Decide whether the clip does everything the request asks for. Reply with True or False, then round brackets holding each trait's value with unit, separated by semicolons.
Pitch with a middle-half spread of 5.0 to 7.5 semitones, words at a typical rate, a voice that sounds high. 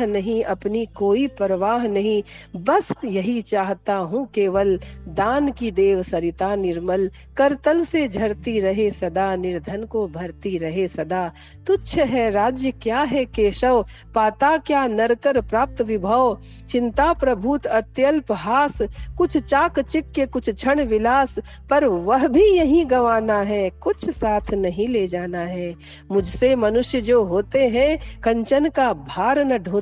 True (5.4 semitones; 135 wpm; 225 Hz)